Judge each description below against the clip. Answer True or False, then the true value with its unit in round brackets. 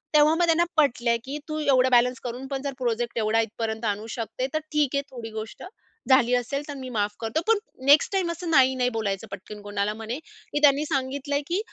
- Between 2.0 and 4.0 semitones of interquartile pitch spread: False (4.5 semitones)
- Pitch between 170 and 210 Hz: False (260 Hz)